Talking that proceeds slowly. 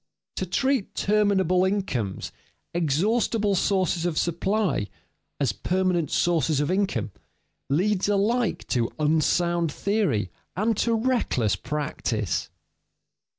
Yes: slow, 100 wpm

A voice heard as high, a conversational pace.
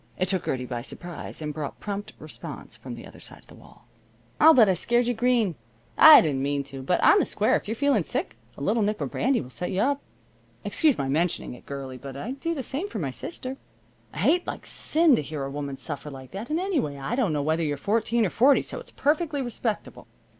No: high, 205 Hz; fast, 240 wpm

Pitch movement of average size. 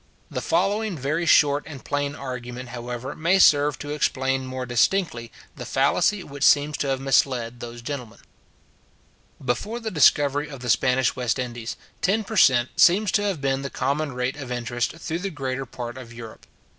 Yes: average, 3.5 semitones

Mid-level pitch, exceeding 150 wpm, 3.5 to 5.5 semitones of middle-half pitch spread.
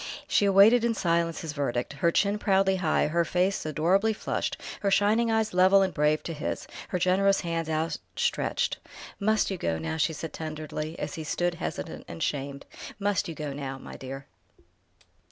Yes: medium, 170 Hz; average, 175 wpm; average, 4.5 semitones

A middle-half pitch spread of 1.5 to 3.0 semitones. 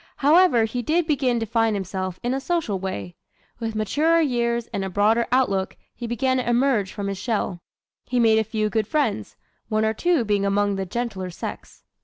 No: average, 4.1 semitones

